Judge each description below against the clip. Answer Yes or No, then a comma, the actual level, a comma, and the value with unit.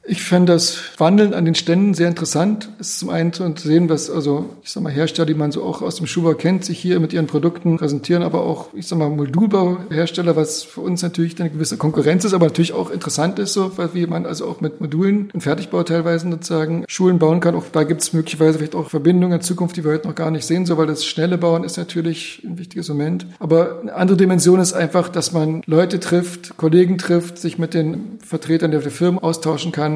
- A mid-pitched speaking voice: Yes, medium, 170 Hz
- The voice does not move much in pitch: Yes, narrow, 1.9 semitones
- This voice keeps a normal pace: No, fast, 230 wpm